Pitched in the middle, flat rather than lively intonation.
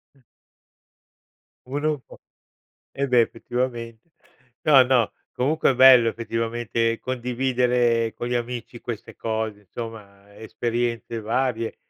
No: low, 120 Hz; narrow, 1.9 semitones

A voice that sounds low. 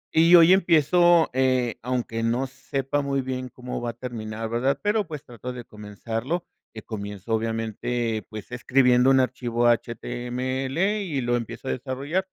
Yes: low, 125 Hz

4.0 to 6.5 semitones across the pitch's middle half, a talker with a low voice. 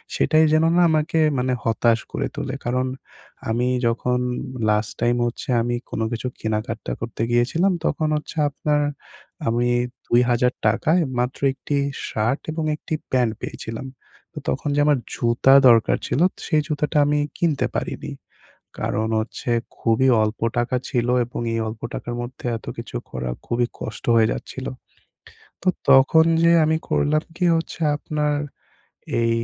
Yes: average, 4.3 semitones; low, 125 Hz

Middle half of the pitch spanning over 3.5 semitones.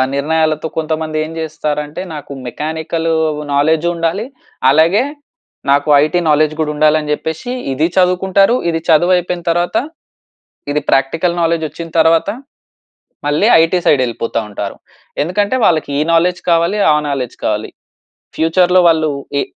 No: narrow, 2.4 semitones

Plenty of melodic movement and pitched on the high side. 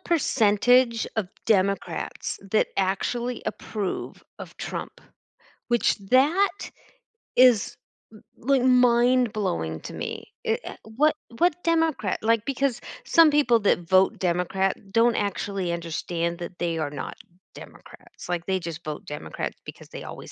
Yes: wide, 5.8 semitones; high, 215 Hz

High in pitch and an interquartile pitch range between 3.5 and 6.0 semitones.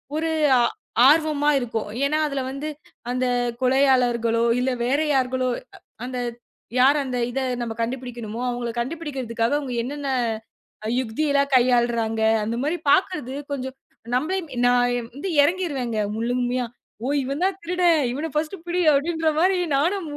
Yes: very high, 260 Hz; average, 3.8 semitones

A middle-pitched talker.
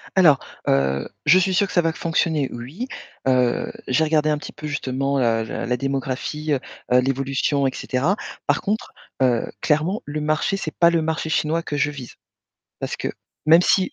Yes: medium, 150 Hz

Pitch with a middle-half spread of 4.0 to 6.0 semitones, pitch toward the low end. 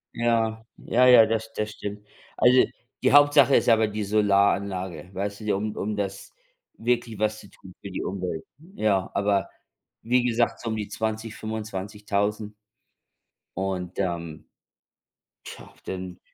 No: narrow, 2.4 semitones; low, 105 Hz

